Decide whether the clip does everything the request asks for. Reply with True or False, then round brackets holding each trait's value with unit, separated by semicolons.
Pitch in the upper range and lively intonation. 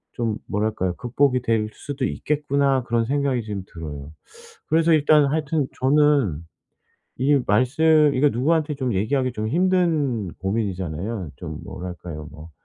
False (125 Hz; 6.3 semitones)